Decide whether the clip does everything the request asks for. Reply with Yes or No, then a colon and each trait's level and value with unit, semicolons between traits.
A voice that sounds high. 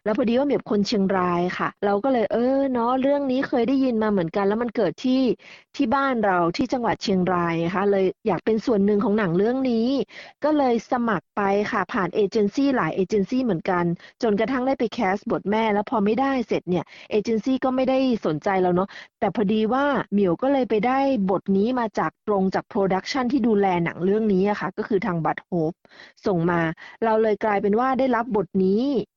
Yes: high, 215 Hz